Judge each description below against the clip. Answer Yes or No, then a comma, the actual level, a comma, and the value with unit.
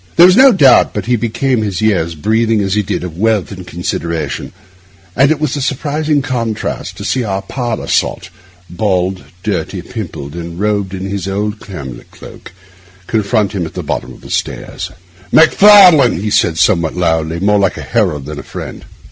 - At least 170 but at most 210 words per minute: Yes, average, 175 wpm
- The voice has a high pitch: No, low, 100 Hz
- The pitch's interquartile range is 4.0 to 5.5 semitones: Yes, average, 4.9 semitones